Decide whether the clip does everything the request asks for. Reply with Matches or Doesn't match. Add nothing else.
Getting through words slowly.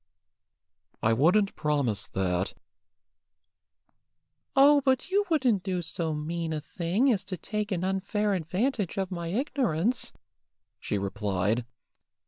Matches